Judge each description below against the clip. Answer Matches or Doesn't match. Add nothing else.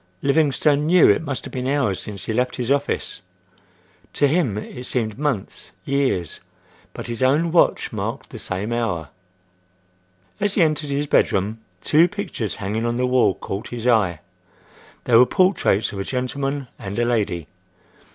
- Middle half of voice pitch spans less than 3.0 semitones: Doesn't match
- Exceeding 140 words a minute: Matches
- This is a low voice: Matches